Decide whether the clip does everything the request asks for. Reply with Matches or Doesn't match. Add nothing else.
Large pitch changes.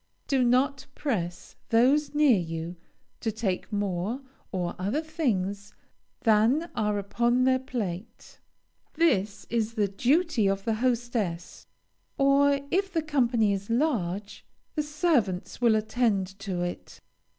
Matches